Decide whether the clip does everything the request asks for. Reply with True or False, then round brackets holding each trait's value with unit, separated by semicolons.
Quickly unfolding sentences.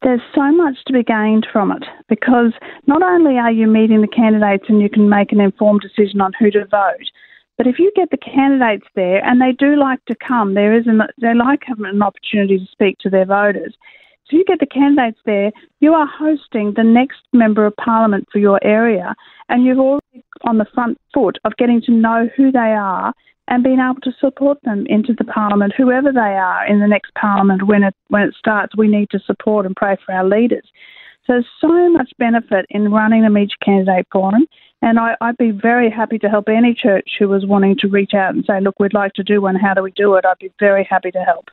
True (230 wpm)